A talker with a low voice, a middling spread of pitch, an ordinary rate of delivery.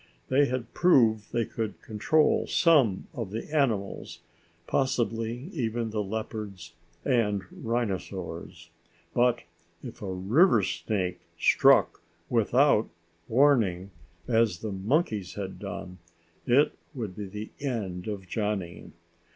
No: low, 110 Hz; average, 3.9 semitones; slow, 110 wpm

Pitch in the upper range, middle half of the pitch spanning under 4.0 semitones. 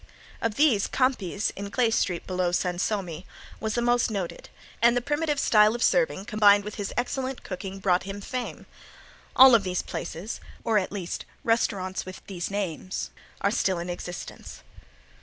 No: high, 205 Hz; average, 4.3 semitones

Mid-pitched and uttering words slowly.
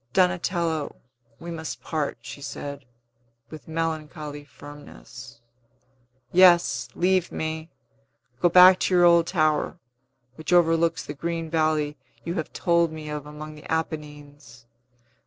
Yes: medium, 160 Hz; slow, 120 wpm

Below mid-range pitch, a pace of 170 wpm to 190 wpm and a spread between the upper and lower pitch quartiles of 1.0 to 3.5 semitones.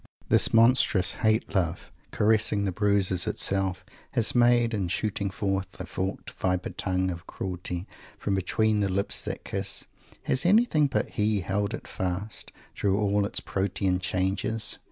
No: low, 100 Hz; average, 150 wpm; narrow, 2.6 semitones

